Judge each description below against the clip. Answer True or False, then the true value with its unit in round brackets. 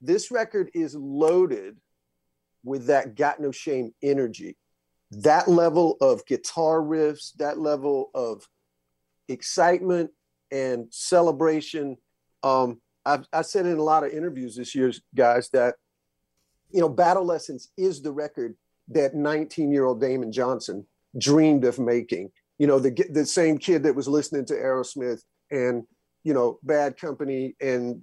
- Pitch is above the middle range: False (140 Hz)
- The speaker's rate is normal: True (145 wpm)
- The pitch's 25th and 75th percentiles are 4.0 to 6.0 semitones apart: True (4.7 semitones)